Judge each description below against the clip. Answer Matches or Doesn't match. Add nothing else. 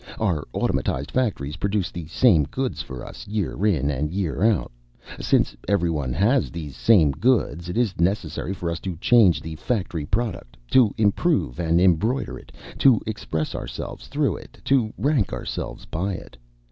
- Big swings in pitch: Matches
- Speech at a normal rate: Matches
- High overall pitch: Doesn't match